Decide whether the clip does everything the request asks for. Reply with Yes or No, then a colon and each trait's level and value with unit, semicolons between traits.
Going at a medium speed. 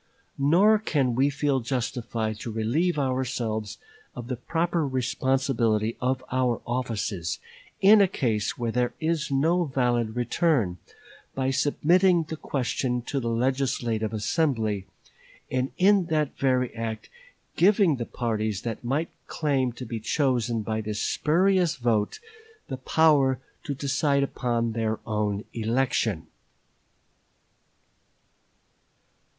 No: slow, 120 wpm